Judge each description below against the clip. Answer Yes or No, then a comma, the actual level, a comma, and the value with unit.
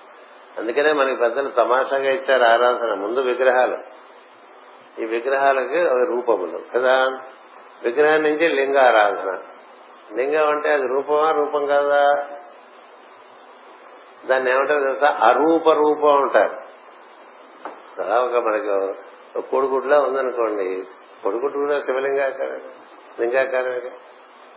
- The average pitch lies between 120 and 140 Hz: Yes, low, 135 Hz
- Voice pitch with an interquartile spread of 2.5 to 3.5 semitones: Yes, average, 2.9 semitones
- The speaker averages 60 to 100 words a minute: Yes, average, 90 wpm